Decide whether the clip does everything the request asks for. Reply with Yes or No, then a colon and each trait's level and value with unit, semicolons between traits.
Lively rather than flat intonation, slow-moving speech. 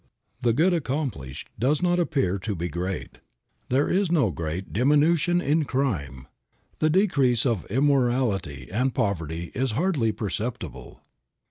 Yes: wide, 7.5 semitones; slow, 130 wpm